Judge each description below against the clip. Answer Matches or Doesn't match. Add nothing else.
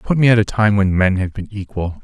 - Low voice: Matches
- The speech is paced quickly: Matches